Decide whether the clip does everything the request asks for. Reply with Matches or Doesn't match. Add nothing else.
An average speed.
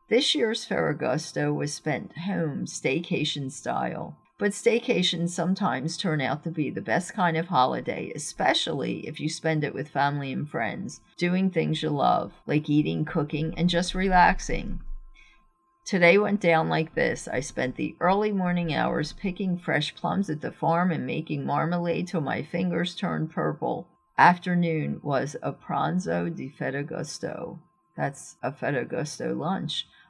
Matches